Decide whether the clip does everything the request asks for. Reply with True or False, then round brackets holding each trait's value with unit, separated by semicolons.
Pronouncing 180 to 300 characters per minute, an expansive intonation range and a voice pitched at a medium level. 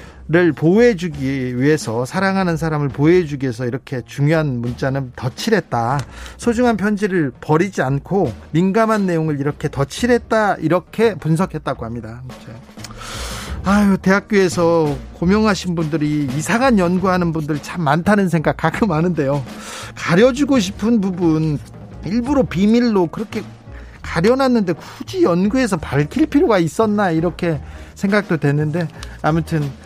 False (310 characters per minute; 5.9 semitones; 170 Hz)